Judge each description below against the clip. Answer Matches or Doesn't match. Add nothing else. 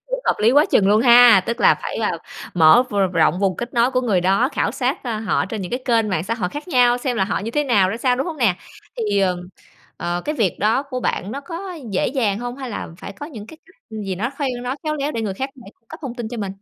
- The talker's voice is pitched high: Matches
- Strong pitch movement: Doesn't match